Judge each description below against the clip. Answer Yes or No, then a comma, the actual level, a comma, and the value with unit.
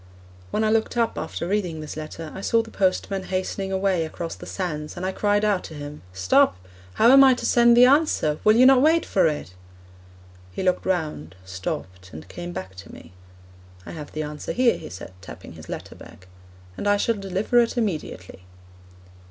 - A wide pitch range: Yes, wide, 6.5 semitones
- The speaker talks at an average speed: Yes, average, 195 wpm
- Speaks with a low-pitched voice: No, medium, 185 Hz